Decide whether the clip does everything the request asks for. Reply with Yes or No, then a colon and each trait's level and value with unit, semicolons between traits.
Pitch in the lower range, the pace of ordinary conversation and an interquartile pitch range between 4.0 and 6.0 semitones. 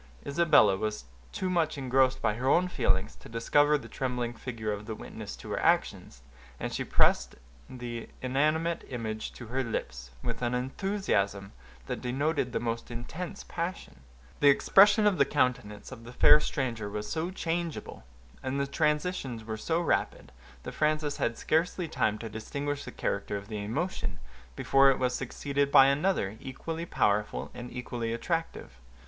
Yes: low, 130 Hz; average, 165 wpm; wide, 5.5 semitones